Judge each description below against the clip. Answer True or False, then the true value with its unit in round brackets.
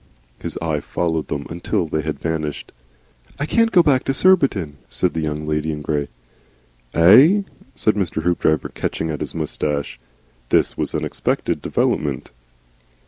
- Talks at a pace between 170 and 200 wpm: False (150 wpm)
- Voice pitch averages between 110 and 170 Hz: False (80 Hz)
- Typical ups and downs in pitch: False (6.0 semitones)